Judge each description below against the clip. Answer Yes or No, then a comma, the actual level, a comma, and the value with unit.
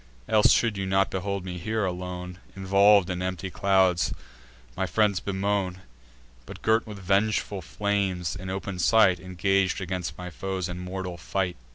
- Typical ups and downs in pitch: No, narrow, 1.6 semitones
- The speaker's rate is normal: Yes, average, 155 wpm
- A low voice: Yes, very low, 95 Hz